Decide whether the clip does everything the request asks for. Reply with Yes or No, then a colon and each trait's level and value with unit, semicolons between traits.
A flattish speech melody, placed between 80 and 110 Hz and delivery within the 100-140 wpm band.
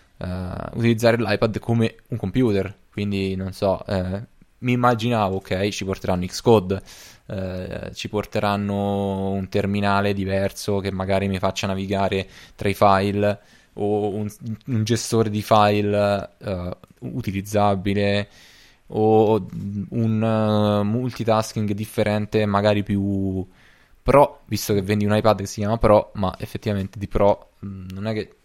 Yes: narrow, 1.8 semitones; low, 105 Hz; average, 135 wpm